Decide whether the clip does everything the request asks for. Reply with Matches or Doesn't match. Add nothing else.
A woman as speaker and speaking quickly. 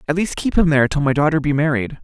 Doesn't match